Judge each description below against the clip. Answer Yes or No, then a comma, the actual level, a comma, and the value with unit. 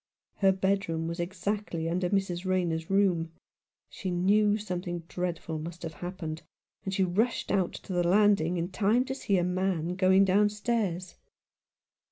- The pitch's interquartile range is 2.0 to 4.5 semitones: Yes, narrow, 2.5 semitones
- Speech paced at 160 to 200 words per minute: No, average, 150 wpm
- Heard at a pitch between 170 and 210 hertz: Yes, medium, 185 Hz